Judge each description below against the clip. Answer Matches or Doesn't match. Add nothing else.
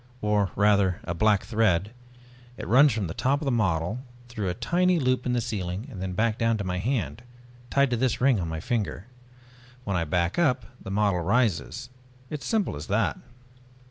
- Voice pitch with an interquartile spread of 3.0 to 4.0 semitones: Doesn't match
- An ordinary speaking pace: Matches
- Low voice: Matches